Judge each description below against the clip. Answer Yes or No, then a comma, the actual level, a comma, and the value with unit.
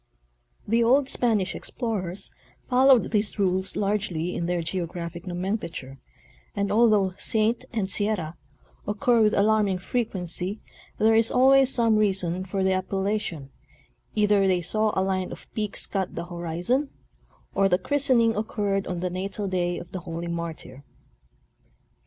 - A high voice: Yes, high, 195 Hz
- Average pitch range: Yes, average, 3.4 semitones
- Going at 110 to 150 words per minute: Yes, average, 140 wpm